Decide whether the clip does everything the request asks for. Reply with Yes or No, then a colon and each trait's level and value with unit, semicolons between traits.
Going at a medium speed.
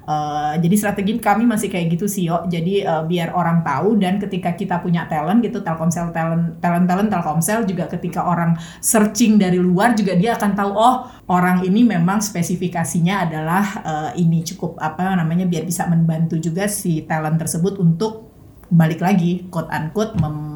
No: fast, 170 wpm